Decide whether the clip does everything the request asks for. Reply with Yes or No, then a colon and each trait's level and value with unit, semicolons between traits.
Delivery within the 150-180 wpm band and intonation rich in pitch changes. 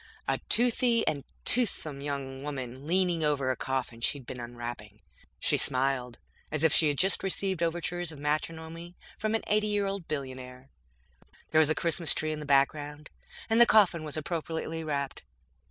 No: average, 165 wpm; average, 4.2 semitones